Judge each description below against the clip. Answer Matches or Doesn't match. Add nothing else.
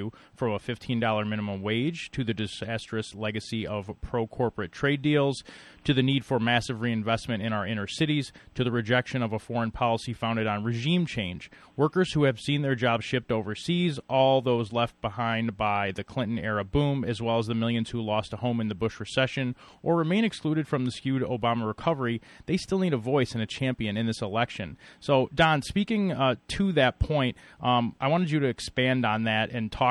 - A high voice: Doesn't match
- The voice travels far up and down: Doesn't match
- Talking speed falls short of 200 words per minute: Doesn't match